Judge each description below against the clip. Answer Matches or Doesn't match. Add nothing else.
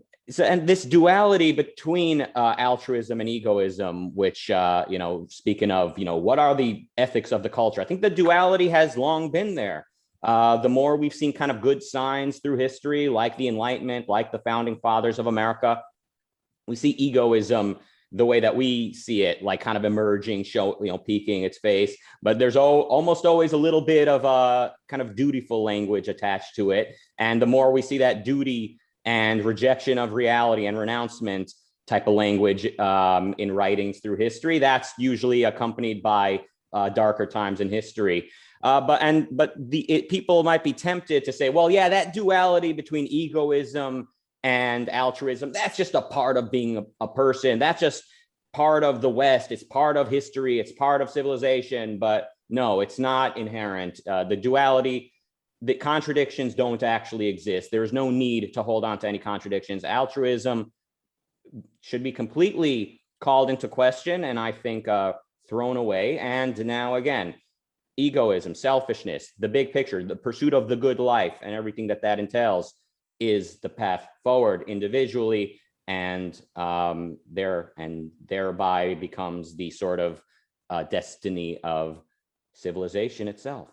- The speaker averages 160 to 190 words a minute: Matches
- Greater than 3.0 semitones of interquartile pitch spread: Matches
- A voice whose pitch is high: Doesn't match